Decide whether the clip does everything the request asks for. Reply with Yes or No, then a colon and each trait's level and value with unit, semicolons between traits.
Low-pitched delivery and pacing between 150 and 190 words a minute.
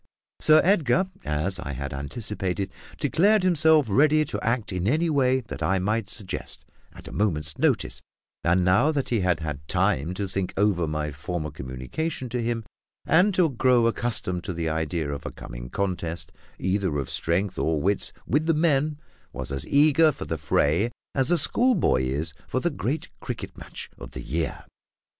Yes: low, 100 Hz; average, 175 wpm